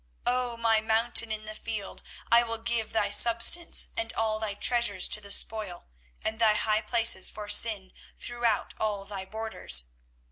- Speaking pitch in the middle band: No, high, 220 Hz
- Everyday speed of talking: Yes, average, 170 wpm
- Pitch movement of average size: No, narrow, 1.9 semitones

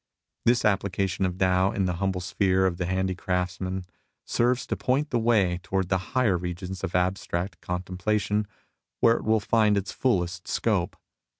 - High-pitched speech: No, very low, 95 Hz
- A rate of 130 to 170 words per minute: Yes, average, 165 wpm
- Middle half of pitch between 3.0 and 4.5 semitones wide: No, narrow, 2.6 semitones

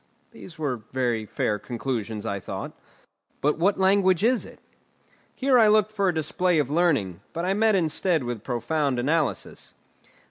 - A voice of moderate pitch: Yes, medium, 155 Hz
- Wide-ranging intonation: Yes, wide, 7.7 semitones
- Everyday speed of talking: Yes, average, 155 wpm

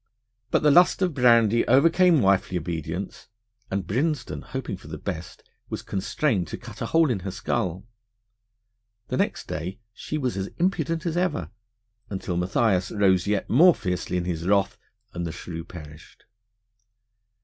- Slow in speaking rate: No, average, 155 wpm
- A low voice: Yes, low, 100 Hz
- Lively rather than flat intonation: Yes, wide, 7.4 semitones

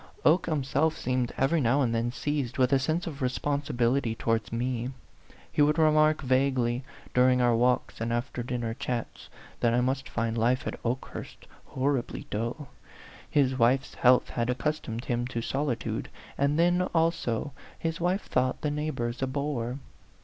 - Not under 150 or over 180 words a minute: Yes, average, 155 wpm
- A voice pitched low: Yes, low, 130 Hz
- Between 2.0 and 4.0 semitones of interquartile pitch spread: Yes, average, 3.5 semitones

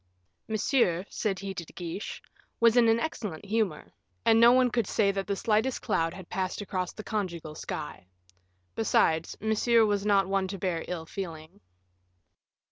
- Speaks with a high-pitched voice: Yes, high, 195 Hz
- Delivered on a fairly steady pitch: No, average, 3.8 semitones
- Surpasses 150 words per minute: Yes, average, 165 wpm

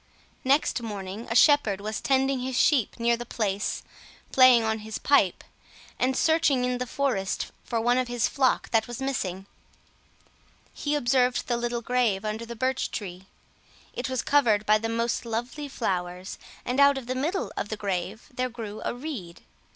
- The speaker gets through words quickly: No, average, 175 wpm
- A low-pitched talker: No, high, 240 Hz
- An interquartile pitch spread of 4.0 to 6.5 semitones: No, average, 3.4 semitones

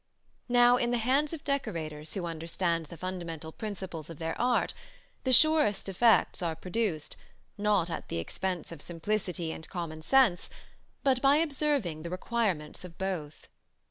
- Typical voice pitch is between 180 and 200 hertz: Yes, medium, 185 Hz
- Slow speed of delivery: No, average, 150 wpm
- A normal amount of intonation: No, wide, 6.7 semitones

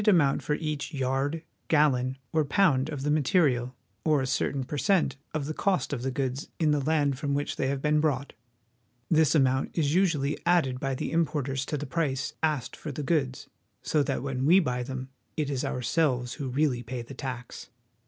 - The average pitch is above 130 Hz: Yes, medium, 140 Hz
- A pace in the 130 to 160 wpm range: No, average, 195 wpm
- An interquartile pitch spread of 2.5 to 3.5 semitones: Yes, average, 2.9 semitones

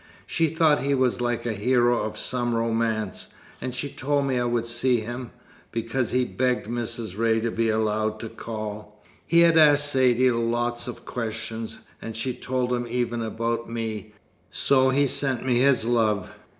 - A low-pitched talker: Yes, low, 120 Hz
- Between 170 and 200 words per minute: Yes, average, 175 wpm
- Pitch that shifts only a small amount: Yes, narrow, 2.3 semitones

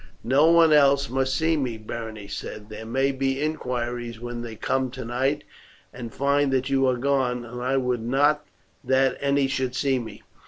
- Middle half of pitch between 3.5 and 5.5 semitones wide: No, narrow, 2.5 semitones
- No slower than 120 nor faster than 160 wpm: No, average, 180 wpm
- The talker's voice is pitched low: Yes, low, 130 Hz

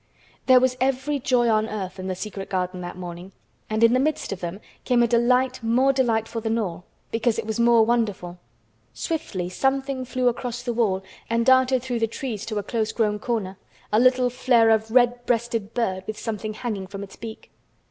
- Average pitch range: Yes, average, 3.3 semitones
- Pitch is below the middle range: No, high, 230 Hz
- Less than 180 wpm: No, average, 200 wpm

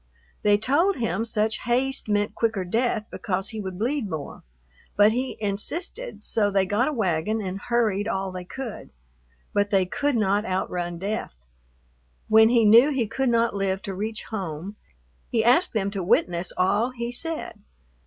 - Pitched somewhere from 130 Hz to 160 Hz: No, high, 215 Hz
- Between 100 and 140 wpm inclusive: No, average, 165 wpm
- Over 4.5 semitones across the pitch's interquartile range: No, average, 3.6 semitones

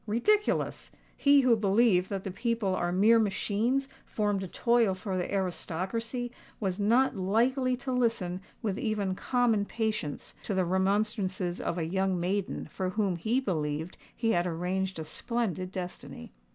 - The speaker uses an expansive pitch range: No, average, 4.0 semitones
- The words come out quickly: No, average, 150 wpm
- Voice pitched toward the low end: No, high, 200 Hz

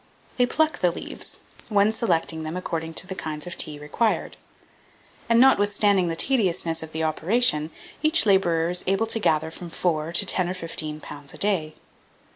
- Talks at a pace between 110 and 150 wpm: No, average, 175 wpm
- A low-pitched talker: No, medium, 175 Hz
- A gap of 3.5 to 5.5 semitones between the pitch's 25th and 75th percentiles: Yes, average, 4.4 semitones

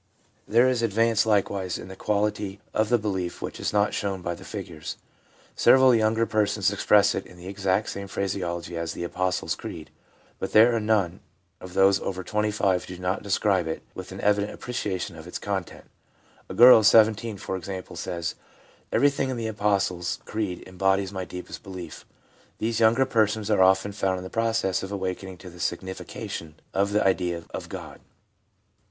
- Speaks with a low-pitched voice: Yes, low, 100 Hz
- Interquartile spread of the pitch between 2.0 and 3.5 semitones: Yes, average, 2.7 semitones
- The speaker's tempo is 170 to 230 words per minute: Yes, average, 185 wpm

